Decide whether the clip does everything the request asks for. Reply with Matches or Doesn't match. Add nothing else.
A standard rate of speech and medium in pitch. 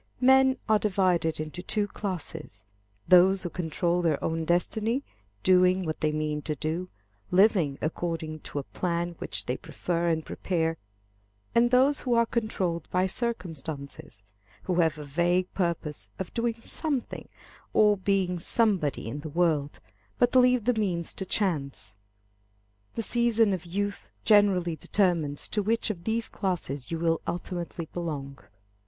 Matches